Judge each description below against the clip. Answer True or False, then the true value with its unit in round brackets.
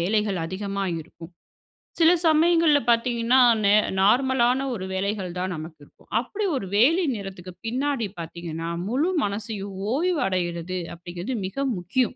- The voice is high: True (205 Hz)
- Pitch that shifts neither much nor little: False (6.2 semitones)